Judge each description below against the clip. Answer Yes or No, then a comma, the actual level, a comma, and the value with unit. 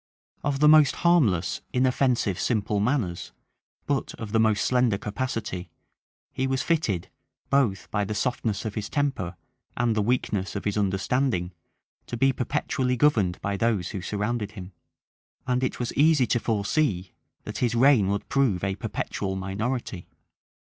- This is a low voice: Yes, low, 110 Hz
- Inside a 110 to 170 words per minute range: Yes, average, 150 wpm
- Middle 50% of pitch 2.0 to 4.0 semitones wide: No, average, 4.6 semitones